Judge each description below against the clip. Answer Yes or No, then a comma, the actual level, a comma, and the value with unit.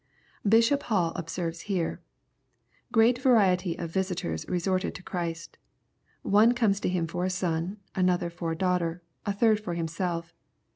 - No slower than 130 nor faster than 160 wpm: Yes, average, 155 wpm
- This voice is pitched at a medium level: Yes, medium, 180 Hz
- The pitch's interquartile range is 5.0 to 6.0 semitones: No, average, 3.0 semitones